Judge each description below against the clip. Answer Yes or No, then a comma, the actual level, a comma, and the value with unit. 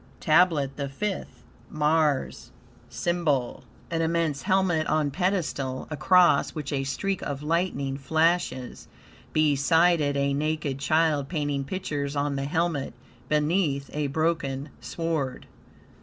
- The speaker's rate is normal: No, slow, 115 wpm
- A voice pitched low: No, medium, 150 Hz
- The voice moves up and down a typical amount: Yes, average, 3.1 semitones